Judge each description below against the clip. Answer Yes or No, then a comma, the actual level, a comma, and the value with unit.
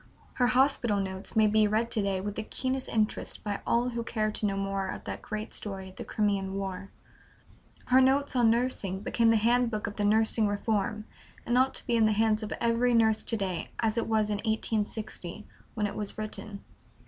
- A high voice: Yes, high, 215 Hz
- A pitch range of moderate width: No, narrow, 2.2 semitones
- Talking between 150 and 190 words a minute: No, fast, 205 wpm